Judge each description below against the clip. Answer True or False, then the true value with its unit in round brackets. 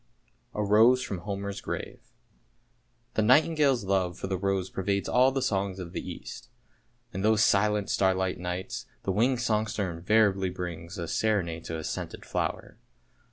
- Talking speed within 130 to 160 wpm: True (155 wpm)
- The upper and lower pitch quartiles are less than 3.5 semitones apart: True (2.8 semitones)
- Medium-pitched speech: False (100 Hz)